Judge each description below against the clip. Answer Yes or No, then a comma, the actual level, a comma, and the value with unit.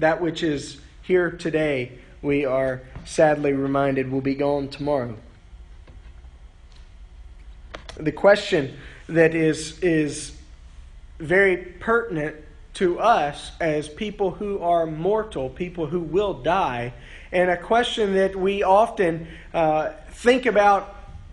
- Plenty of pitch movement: Yes, wide, 5.7 semitones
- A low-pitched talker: No, medium, 155 Hz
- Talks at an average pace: No, slow, 115 wpm